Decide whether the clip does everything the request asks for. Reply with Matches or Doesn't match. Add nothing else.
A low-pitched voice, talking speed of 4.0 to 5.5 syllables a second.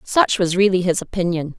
Doesn't match